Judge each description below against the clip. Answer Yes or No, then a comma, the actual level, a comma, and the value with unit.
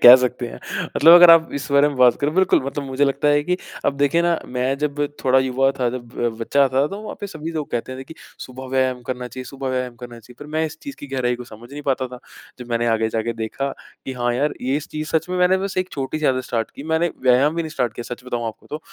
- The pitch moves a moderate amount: Yes, average, 3.5 semitones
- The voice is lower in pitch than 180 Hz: Yes, low, 135 Hz